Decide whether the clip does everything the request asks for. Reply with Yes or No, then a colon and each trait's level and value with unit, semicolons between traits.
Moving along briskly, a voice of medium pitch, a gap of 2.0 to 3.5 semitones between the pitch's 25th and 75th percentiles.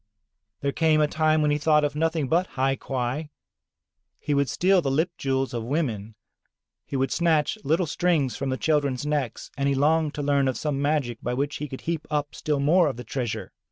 Yes: fast, 210 wpm; medium, 145 Hz; average, 2.7 semitones